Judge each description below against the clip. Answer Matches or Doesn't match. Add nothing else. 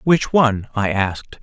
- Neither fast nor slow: Matches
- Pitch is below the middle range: Matches